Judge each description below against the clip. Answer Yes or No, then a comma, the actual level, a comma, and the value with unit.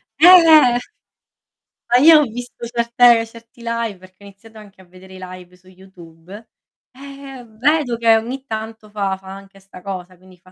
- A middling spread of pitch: Yes, average, 4.4 semitones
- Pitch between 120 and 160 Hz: No, high, 220 Hz